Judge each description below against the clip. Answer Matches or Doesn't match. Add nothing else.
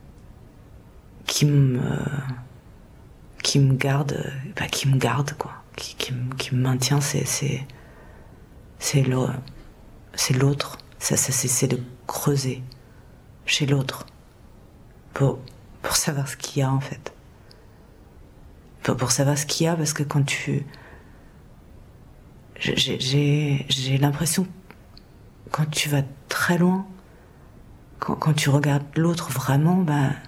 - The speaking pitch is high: Doesn't match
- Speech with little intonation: Matches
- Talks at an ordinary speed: Doesn't match